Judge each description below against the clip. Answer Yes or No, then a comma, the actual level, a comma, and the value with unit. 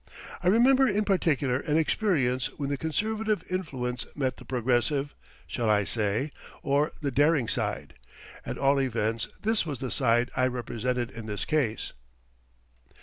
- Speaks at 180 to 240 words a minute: No, average, 145 wpm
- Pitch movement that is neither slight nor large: Yes, average, 4.9 semitones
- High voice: No, low, 135 Hz